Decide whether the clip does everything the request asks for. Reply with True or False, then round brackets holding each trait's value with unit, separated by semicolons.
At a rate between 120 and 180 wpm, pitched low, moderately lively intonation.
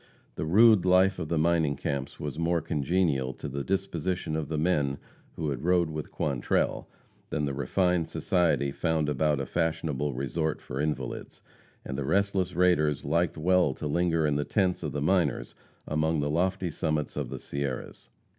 True (175 wpm; 80 Hz; 3.5 semitones)